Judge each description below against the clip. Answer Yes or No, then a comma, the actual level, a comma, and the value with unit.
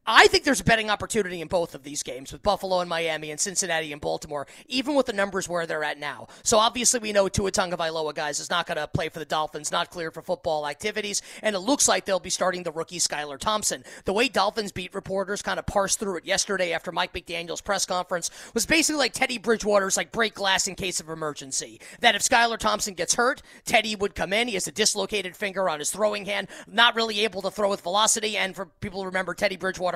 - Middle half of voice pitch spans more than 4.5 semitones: No, average, 3.9 semitones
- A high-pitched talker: Yes, high, 195 Hz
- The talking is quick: Yes, fast, 235 wpm